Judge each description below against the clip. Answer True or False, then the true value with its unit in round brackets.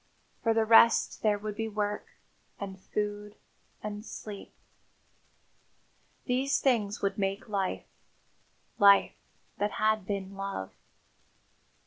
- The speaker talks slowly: True (105 wpm)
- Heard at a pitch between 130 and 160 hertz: False (205 Hz)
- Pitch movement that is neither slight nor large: False (1.5 semitones)